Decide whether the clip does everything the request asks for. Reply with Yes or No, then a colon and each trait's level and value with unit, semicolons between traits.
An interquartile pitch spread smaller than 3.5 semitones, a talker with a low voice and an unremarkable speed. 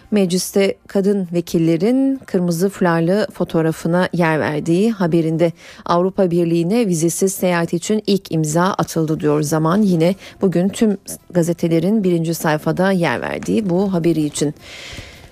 No: average, 2.8 semitones; medium, 175 Hz; average, 120 wpm